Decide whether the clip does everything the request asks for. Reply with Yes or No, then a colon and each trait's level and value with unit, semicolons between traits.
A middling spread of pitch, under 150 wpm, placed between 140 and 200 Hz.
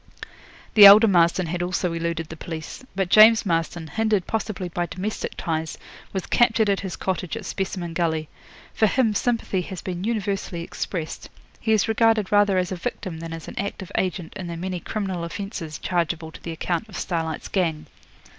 No: average, 3.5 semitones; average, 180 wpm; medium, 185 Hz